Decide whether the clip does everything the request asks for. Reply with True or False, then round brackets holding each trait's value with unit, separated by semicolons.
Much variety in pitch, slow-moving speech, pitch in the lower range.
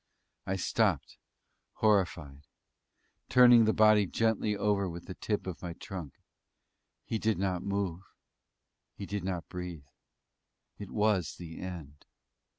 False (3.3 semitones; 125 wpm; 95 Hz)